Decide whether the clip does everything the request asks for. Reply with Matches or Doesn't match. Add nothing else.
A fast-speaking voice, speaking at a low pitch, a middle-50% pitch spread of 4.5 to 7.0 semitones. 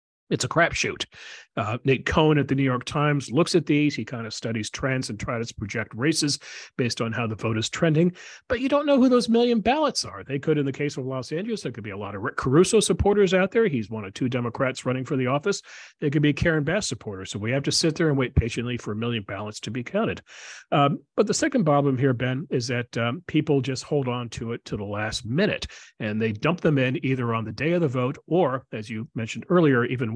Matches